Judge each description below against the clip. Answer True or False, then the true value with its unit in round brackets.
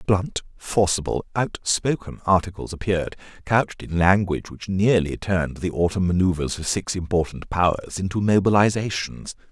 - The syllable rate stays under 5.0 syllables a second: False (5.1 syllables/s)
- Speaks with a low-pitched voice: True (95 Hz)